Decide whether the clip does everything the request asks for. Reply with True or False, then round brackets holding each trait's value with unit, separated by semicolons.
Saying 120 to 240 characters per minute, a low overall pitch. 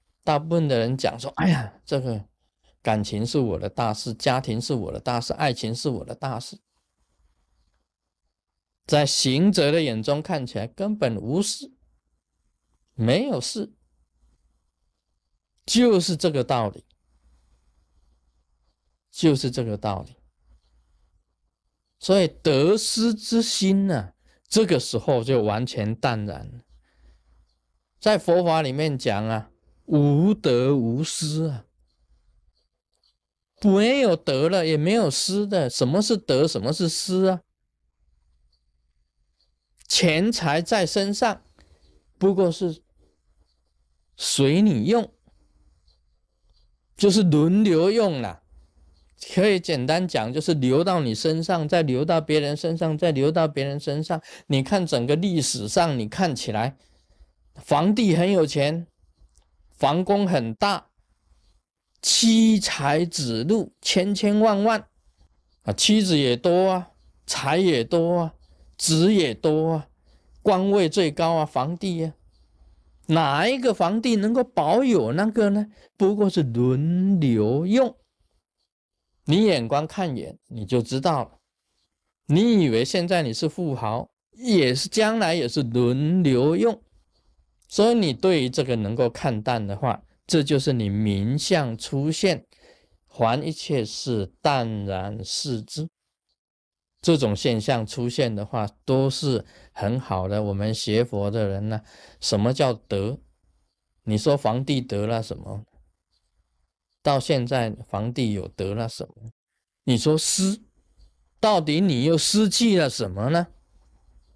True (175 characters per minute; 130 Hz)